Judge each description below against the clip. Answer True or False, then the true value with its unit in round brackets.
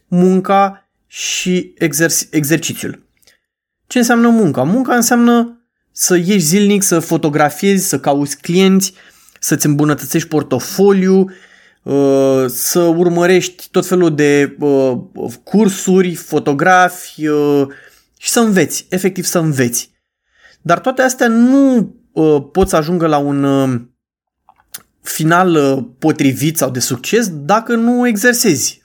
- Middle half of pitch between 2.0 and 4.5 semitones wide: False (5.1 semitones)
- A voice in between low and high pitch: True (175 Hz)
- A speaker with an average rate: False (100 wpm)